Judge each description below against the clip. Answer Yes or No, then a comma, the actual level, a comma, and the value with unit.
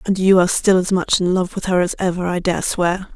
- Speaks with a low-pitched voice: No, medium, 185 Hz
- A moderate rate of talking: No, fast, 285 wpm